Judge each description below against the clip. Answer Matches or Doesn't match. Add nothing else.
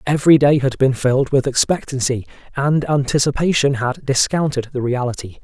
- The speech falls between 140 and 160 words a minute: Matches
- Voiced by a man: Matches